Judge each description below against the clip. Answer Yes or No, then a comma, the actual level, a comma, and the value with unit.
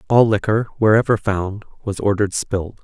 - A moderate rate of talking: Yes, average, 150 wpm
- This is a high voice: No, low, 105 Hz